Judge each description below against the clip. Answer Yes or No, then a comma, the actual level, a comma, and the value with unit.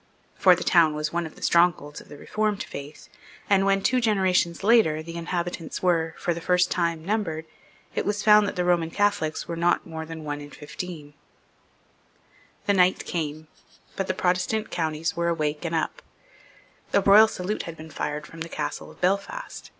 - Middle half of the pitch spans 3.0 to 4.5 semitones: Yes, average, 3.4 semitones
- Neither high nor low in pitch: Yes, medium, 170 Hz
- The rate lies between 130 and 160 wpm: No, average, 185 wpm